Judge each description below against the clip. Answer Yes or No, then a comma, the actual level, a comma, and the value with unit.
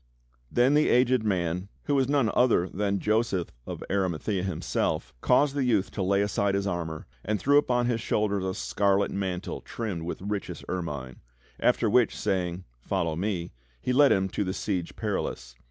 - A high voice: No, low, 100 Hz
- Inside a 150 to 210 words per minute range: Yes, average, 175 wpm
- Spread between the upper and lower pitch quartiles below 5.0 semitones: Yes, average, 4.6 semitones